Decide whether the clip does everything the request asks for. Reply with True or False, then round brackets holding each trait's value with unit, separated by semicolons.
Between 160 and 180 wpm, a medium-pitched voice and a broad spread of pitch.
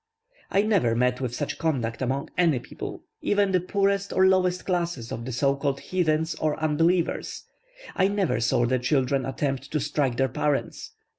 True (170 wpm; 150 Hz; 5.9 semitones)